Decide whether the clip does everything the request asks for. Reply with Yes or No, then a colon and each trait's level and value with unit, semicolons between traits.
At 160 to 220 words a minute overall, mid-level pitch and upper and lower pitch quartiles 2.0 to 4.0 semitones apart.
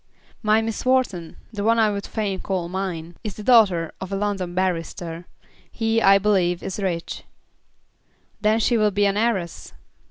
No: average, 165 wpm; high, 200 Hz; average, 3.4 semitones